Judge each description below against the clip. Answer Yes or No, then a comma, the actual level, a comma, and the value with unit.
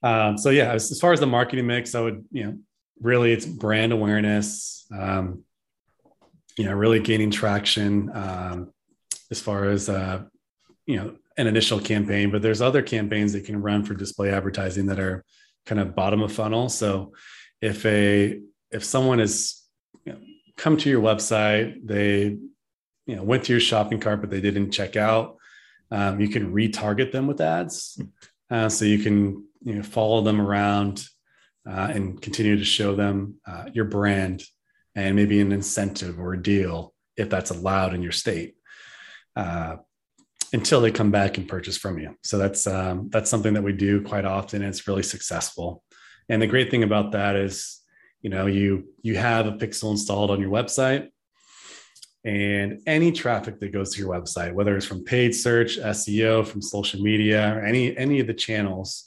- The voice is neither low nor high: No, low, 105 Hz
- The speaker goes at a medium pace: Yes, average, 180 wpm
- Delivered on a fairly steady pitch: Yes, narrow, 2.0 semitones